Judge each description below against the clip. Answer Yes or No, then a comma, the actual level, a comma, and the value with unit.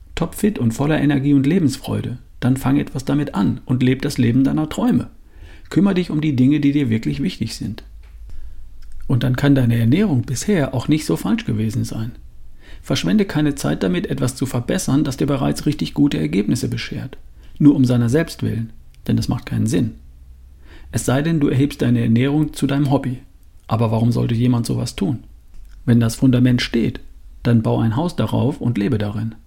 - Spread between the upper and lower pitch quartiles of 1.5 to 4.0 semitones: No, average, 4.8 semitones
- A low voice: Yes, low, 125 Hz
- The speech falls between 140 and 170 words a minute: No, average, 185 wpm